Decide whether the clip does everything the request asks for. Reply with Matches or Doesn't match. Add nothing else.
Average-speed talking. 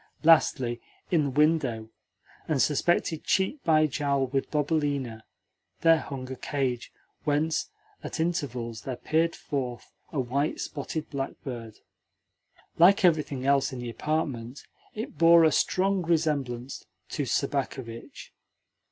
Doesn't match